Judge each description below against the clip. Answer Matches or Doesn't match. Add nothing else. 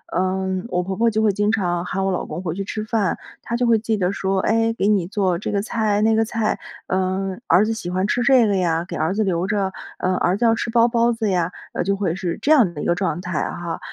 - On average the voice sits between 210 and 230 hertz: Doesn't match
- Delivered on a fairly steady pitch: Doesn't match